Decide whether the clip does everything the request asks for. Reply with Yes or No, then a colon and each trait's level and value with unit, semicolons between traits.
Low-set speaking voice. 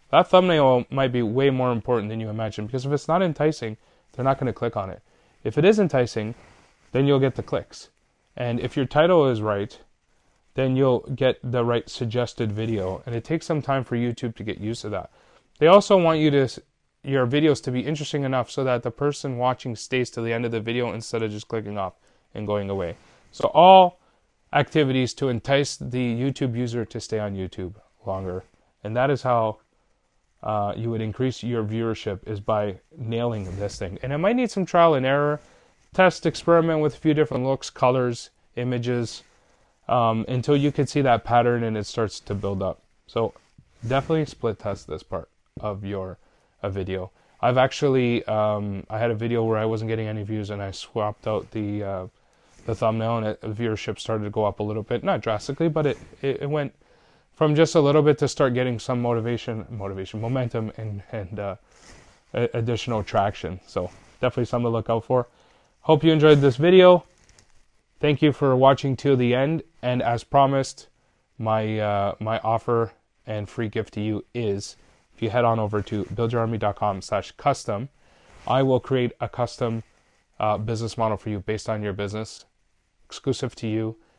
Yes: low, 120 Hz